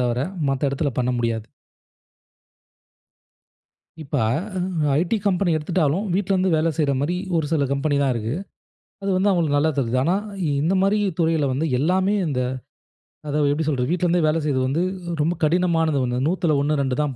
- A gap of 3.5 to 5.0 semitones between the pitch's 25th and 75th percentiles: Yes, average, 4.2 semitones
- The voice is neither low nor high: Yes, medium, 155 Hz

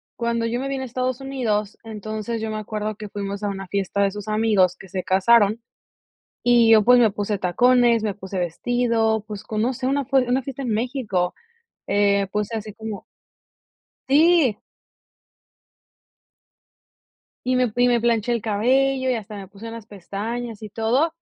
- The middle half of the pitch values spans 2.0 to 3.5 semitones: Yes, average, 3.1 semitones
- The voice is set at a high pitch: Yes, high, 220 Hz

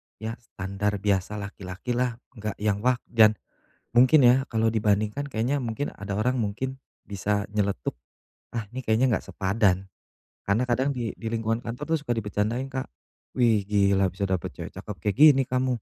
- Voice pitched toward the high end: No, low, 110 Hz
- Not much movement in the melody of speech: No, average, 3.6 semitones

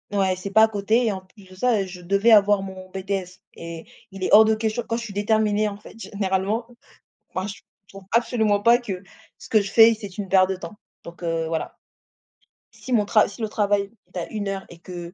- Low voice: No, high, 200 Hz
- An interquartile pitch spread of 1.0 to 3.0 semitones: Yes, narrow, 2.6 semitones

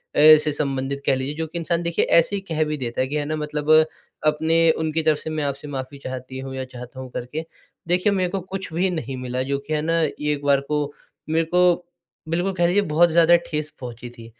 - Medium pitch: Yes, medium, 150 Hz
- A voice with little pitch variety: No, average, 3.6 semitones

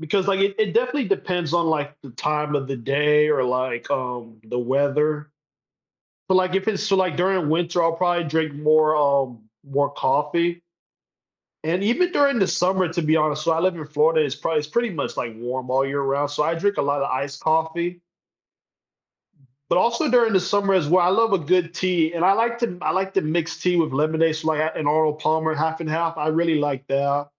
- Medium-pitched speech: Yes, medium, 160 Hz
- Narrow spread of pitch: No, average, 3.9 semitones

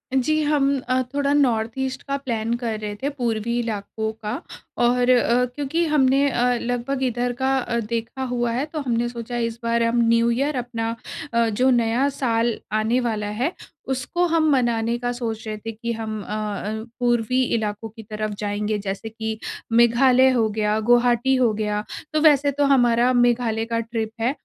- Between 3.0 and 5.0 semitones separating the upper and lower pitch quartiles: No, narrow, 2.6 semitones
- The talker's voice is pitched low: No, high, 235 Hz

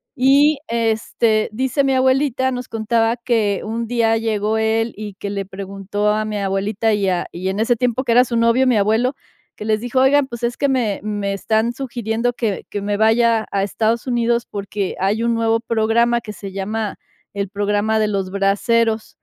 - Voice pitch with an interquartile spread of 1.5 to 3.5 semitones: Yes, narrow, 2.5 semitones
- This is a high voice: Yes, high, 225 Hz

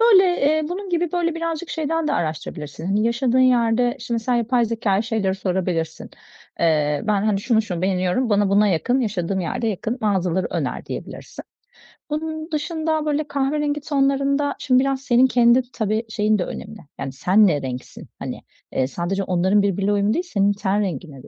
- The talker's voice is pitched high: Yes, high, 220 Hz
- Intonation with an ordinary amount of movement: No, wide, 6.6 semitones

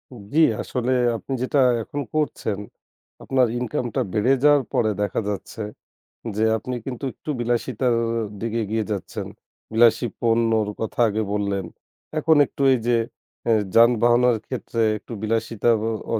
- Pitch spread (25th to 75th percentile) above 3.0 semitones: No, narrow, 2.4 semitones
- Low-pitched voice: Yes, low, 115 Hz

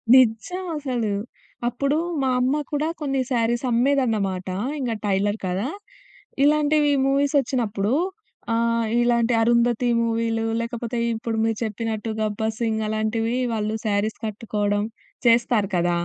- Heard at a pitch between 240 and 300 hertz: No, high, 230 Hz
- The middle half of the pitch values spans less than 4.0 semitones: Yes, narrow, 2.5 semitones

